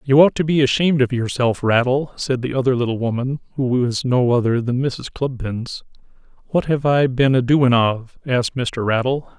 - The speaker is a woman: No, male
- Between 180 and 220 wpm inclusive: Yes, average, 190 wpm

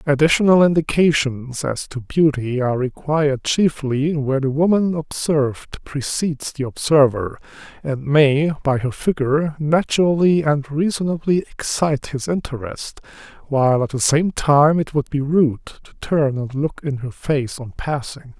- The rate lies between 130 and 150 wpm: Yes, average, 145 wpm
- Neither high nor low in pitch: Yes, medium, 145 Hz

